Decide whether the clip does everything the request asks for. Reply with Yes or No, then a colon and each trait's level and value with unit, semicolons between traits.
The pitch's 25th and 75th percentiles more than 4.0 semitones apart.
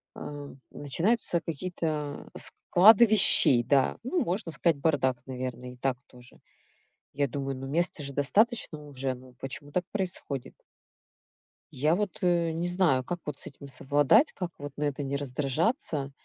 Yes: average, 4.6 semitones